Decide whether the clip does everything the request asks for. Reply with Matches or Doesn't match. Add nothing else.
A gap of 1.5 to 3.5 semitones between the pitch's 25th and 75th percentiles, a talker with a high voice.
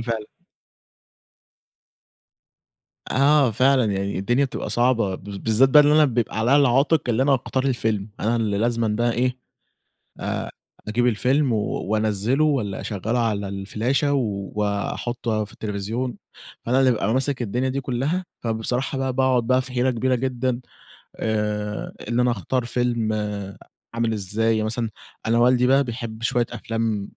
Doesn't match